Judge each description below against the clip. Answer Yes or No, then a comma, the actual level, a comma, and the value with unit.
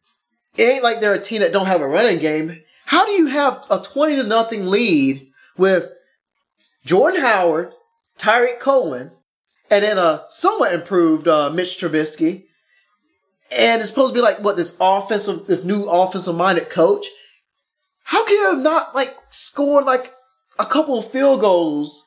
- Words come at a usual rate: Yes, average, 165 wpm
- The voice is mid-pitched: No, high, 225 Hz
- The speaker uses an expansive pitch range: Yes, wide, 7.9 semitones